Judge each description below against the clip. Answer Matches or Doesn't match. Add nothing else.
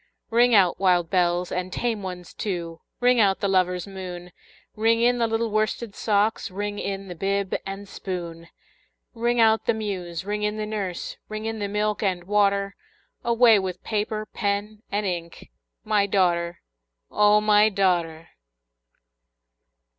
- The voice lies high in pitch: Matches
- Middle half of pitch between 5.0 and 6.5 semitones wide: Doesn't match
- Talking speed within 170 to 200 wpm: Doesn't match